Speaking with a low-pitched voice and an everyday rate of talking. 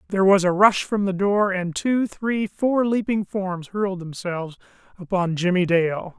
No: high, 190 Hz; average, 175 wpm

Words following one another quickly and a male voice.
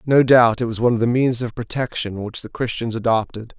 Yes: fast, 235 wpm; male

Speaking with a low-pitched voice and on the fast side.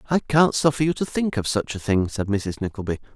Yes: low, 125 Hz; fast, 245 wpm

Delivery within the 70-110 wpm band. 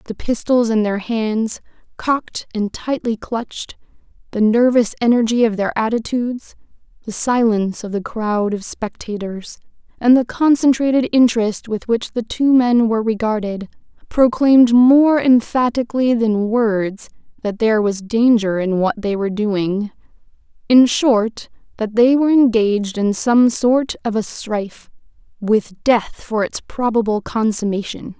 No: slow, 135 wpm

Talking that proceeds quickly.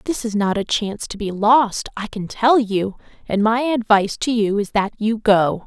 Yes: fast, 220 wpm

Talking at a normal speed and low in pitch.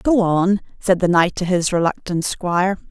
No: average, 185 wpm; medium, 185 Hz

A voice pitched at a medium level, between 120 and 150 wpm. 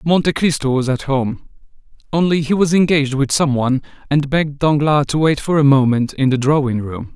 No: medium, 145 Hz; average, 200 wpm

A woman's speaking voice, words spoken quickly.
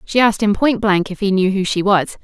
Yes: female; fast, 295 wpm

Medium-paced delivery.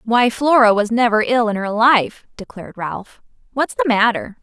Yes: average, 175 wpm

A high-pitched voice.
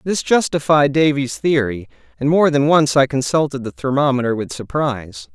No: low, 135 Hz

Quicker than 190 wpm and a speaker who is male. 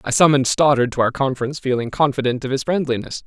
Yes: average, 200 wpm; male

